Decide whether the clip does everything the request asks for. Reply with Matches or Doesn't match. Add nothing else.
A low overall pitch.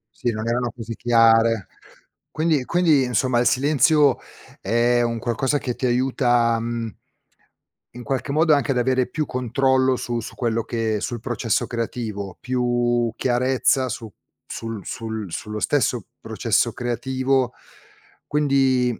Matches